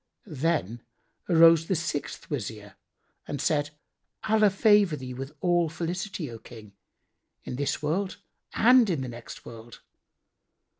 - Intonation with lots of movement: Yes, wide, 6.3 semitones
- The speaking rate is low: Yes, slow, 130 wpm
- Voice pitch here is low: No, medium, 155 Hz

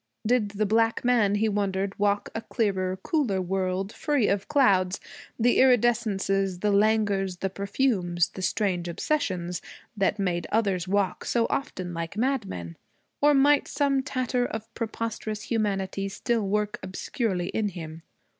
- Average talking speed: Yes, average, 145 wpm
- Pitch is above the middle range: Yes, high, 205 Hz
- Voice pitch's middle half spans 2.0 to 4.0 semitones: Yes, average, 3.4 semitones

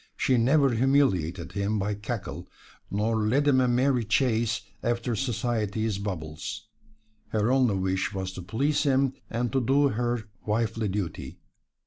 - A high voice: No, low, 115 Hz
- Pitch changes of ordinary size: Yes, average, 4.0 semitones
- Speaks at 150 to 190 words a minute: No, average, 140 wpm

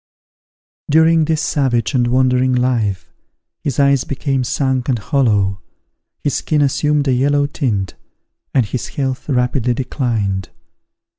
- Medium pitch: No, low, 130 Hz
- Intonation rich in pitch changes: No, average, 2.8 semitones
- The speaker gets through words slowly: Yes, slow, 125 wpm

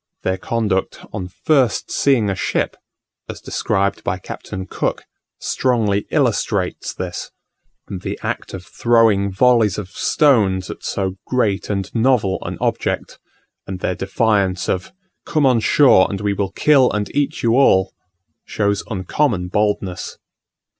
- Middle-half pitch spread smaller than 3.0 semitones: No, average, 3.8 semitones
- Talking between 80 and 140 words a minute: Yes, slow, 135 wpm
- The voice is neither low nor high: No, low, 100 Hz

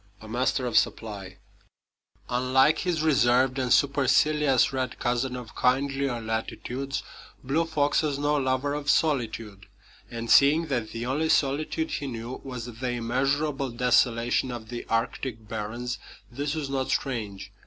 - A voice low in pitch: Yes, low, 130 Hz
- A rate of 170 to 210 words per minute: No, average, 140 wpm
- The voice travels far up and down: No, average, 3.0 semitones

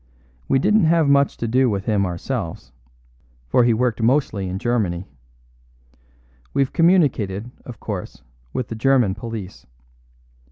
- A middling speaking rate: No, slow, 130 wpm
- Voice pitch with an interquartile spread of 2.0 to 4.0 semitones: No, average, 5.3 semitones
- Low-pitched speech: Yes, low, 115 Hz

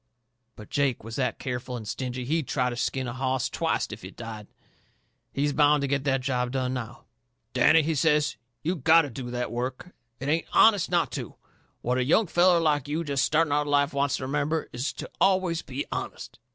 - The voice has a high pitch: No, medium, 140 Hz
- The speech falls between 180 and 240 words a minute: Yes, fast, 205 wpm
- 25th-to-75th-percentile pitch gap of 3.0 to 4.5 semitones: Yes, average, 3.7 semitones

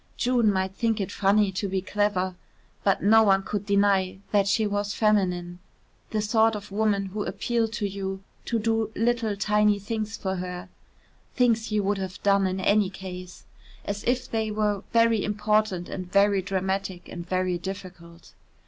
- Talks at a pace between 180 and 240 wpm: No, average, 165 wpm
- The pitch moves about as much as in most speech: No, narrow, 2.1 semitones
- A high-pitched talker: Yes, high, 200 Hz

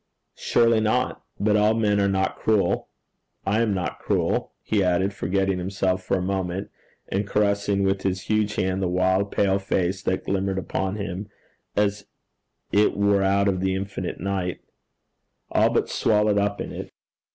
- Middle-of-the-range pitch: No, low, 100 Hz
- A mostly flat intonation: Yes, narrow, 1.4 semitones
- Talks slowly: No, average, 165 wpm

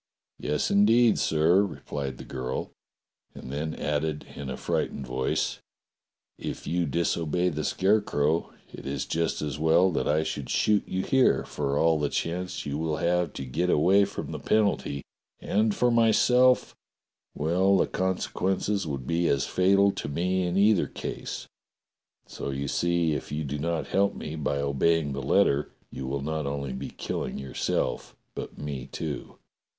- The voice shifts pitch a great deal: No, average, 4.8 semitones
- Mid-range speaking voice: No, very low, 80 Hz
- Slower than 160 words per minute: No, average, 165 wpm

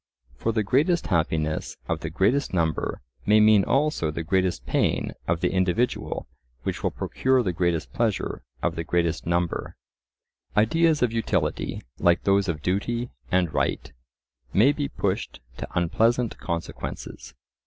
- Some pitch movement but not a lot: No, wide, 5.7 semitones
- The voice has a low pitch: Yes, very low, 95 Hz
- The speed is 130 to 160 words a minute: Yes, average, 145 wpm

